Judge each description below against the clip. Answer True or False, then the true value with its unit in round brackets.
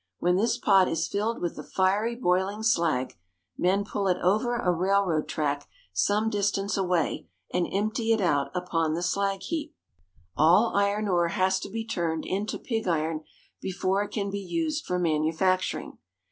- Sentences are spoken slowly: False (165 wpm)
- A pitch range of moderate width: True (3.2 semitones)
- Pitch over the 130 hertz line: True (190 Hz)